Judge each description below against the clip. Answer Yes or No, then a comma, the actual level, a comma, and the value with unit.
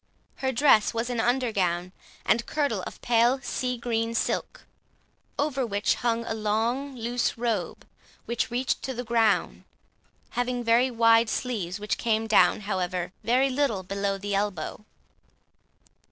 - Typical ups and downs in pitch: Yes, average, 3.0 semitones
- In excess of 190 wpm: No, average, 140 wpm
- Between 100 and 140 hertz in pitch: No, high, 230 Hz